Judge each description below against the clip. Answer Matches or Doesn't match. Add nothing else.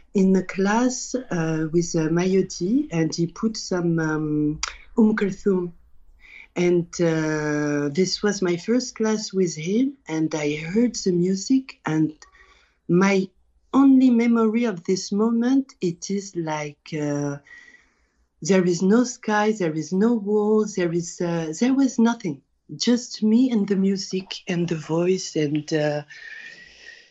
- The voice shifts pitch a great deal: Matches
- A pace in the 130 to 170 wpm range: Matches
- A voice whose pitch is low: Doesn't match